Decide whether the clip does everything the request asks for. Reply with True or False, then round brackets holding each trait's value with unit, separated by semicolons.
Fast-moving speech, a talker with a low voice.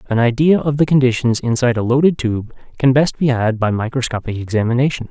False (190 wpm; 125 Hz)